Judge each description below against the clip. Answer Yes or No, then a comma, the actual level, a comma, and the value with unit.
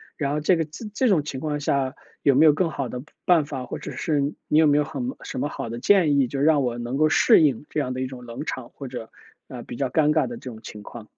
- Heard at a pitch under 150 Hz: Yes, medium, 140 Hz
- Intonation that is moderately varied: Yes, average, 3.4 semitones